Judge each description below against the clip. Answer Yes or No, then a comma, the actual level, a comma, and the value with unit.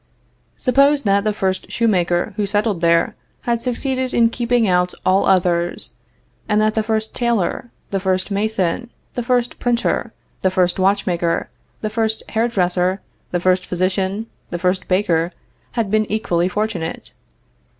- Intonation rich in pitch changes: No, average, 3.8 semitones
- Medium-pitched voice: No, high, 200 Hz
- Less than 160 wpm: Yes, average, 145 wpm